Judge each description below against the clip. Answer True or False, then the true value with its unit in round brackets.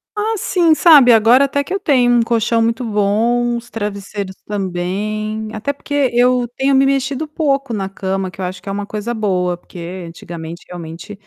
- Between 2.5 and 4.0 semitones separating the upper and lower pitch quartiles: False (5.5 semitones)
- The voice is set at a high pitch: True (220 Hz)